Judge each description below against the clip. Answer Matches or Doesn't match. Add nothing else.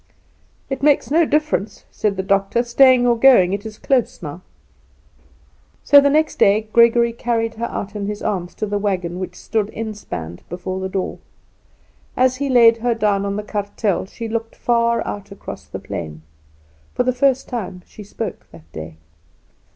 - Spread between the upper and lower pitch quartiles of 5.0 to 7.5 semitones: Doesn't match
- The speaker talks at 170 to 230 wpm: Matches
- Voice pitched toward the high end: Matches